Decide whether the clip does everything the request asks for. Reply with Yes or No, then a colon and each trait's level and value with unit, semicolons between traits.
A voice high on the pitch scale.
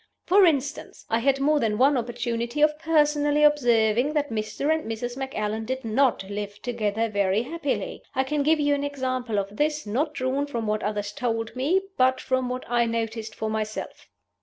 Yes: very high, 250 Hz